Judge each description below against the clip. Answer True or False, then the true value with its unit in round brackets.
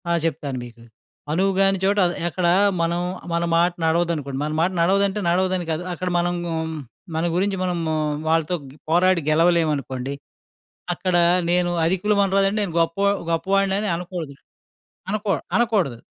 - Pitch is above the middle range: False (175 Hz)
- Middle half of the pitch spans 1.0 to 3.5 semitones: True (2.9 semitones)